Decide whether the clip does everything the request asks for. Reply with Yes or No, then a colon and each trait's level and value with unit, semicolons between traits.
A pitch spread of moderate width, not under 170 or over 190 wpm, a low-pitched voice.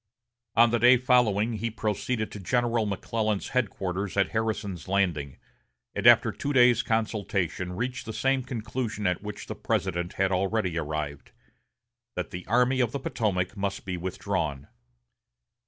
No: average, 4.3 semitones; average, 145 wpm; low, 105 Hz